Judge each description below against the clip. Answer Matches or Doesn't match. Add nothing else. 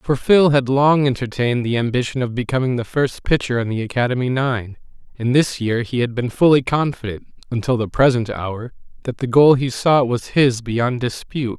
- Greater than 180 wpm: Matches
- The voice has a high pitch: Doesn't match